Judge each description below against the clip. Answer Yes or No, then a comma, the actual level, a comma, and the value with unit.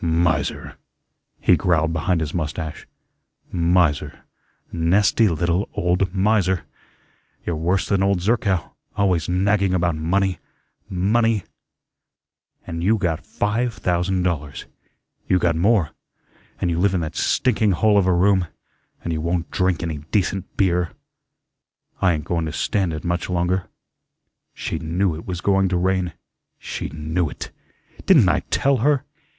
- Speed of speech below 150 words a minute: Yes, average, 140 wpm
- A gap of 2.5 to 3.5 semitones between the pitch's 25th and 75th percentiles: Yes, average, 2.8 semitones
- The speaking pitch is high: No, very low, 90 Hz